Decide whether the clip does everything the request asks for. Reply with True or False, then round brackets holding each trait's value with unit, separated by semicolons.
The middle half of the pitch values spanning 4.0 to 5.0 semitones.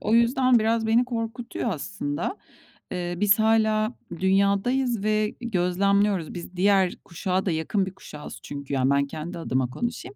True (4.3 semitones)